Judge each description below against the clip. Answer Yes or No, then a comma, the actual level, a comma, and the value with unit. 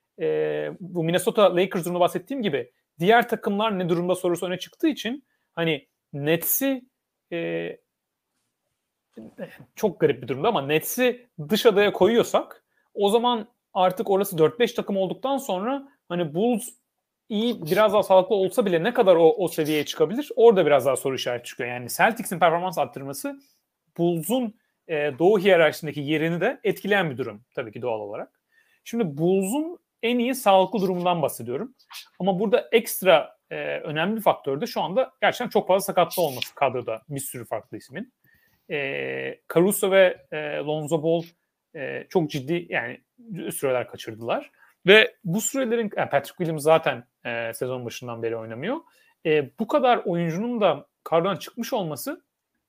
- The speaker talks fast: Yes, fast, 150 wpm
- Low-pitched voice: No, medium, 185 Hz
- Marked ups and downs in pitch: Yes, wide, 6.8 semitones